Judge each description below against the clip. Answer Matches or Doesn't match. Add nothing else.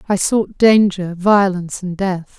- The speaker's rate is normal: Matches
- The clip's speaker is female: Matches